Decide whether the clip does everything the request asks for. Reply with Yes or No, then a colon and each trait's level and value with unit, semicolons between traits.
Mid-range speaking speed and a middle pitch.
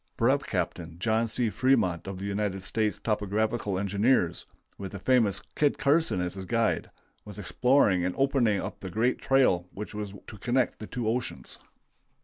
No: average, 165 wpm; low, 105 Hz